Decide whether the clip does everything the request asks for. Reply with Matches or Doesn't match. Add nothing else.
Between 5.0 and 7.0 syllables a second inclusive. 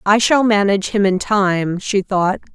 Doesn't match